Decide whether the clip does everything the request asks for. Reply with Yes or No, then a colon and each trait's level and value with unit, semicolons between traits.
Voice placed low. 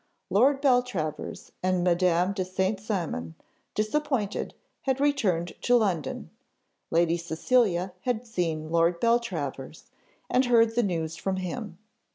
No: high, 190 Hz